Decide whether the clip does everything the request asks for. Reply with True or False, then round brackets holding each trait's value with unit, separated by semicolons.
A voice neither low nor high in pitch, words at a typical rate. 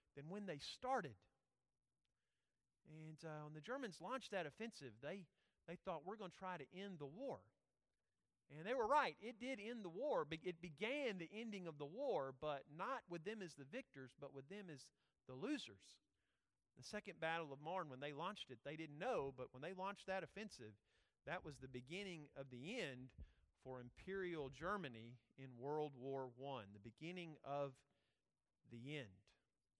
True (155 Hz; 180 wpm)